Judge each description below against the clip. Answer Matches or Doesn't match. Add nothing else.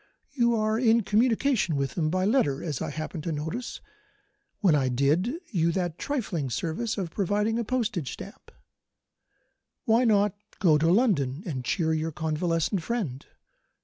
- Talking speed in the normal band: Matches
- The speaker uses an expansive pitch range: Matches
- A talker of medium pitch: Matches